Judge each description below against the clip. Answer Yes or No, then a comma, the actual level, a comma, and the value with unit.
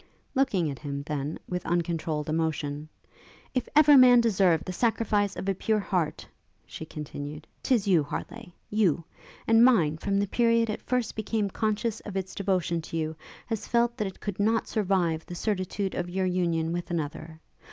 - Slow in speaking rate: No, average, 175 wpm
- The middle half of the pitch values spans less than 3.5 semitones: No, average, 5.2 semitones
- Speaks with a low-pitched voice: No, medium, 185 Hz